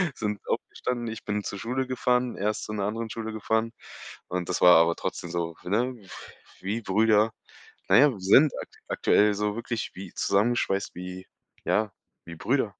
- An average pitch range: Yes, average, 3.2 semitones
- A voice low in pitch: Yes, low, 105 Hz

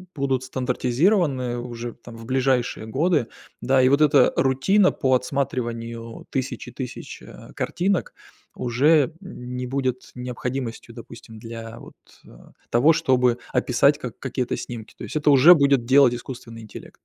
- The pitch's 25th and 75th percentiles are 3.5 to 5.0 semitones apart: No, narrow, 2.6 semitones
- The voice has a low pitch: Yes, low, 130 Hz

